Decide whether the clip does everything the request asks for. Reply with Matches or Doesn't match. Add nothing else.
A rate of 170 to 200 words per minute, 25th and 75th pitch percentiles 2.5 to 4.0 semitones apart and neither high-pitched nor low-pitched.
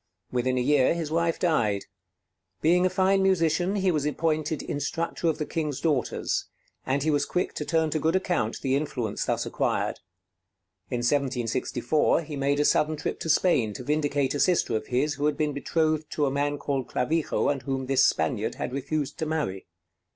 Matches